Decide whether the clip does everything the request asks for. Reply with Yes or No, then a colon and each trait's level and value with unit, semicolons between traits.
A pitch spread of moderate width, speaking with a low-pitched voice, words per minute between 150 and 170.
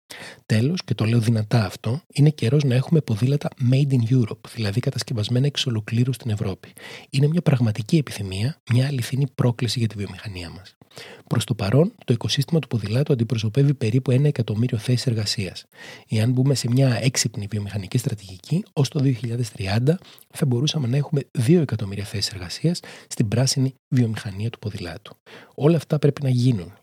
Yes: average, 3.9 semitones; low, 125 Hz; average, 160 wpm